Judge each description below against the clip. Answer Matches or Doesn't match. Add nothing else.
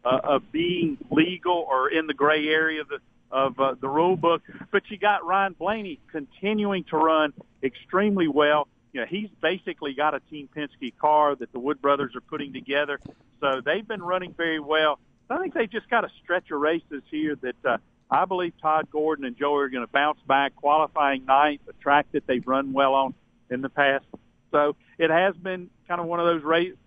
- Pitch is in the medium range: Matches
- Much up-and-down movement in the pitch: Doesn't match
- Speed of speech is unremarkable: Doesn't match